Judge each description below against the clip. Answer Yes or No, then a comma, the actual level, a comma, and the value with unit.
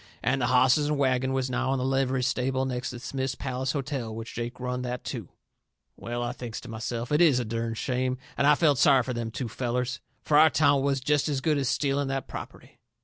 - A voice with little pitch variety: Yes, narrow, 1.9 semitones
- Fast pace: Yes, fast, 230 wpm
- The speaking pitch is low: Yes, low, 130 Hz